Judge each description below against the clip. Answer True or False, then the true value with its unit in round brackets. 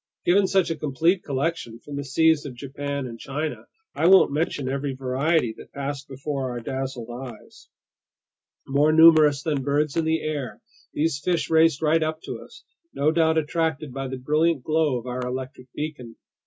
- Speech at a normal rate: True (175 wpm)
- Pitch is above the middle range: False (145 Hz)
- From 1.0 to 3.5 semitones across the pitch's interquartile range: True (3.2 semitones)